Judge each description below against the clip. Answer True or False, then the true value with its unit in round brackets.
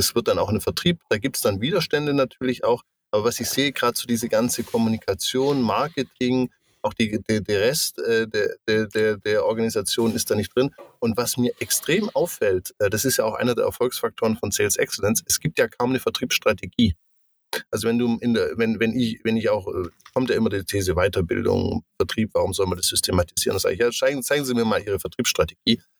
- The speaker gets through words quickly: True (215 wpm)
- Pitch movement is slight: False (3.2 semitones)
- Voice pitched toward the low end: True (120 Hz)